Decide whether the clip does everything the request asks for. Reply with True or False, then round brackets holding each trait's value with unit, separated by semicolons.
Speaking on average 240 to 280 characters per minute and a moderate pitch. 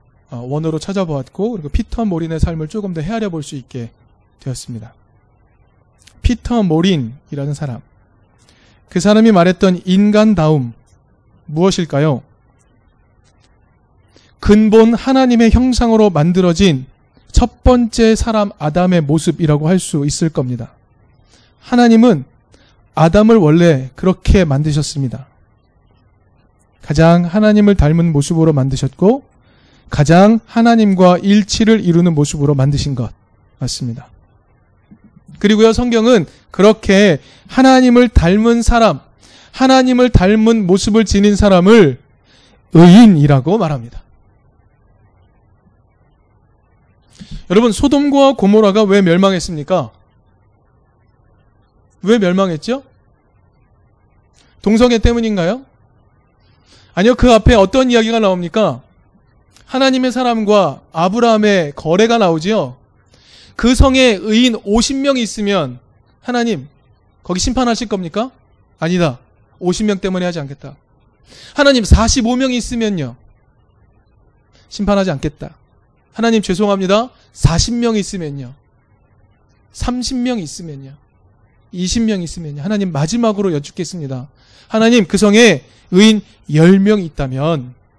True (245 characters per minute; 165 Hz)